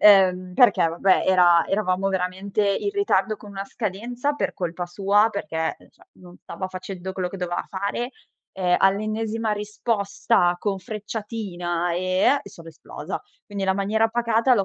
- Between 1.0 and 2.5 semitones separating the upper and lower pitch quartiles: No, average, 2.9 semitones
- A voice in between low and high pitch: No, high, 195 Hz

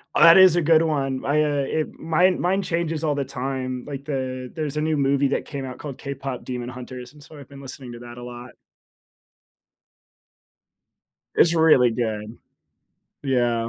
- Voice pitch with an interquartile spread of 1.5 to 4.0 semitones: Yes, average, 3.6 semitones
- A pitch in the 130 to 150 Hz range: Yes, medium, 140 Hz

